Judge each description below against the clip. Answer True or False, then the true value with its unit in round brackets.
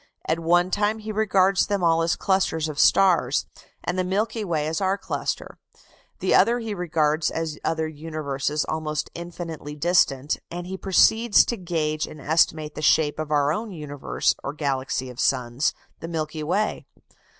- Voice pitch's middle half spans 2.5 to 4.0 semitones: True (3.7 semitones)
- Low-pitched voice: False (160 Hz)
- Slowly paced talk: False (165 wpm)